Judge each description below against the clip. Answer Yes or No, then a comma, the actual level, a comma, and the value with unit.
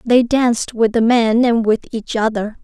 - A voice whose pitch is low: No, high, 230 Hz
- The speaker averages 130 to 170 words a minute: No, fast, 205 wpm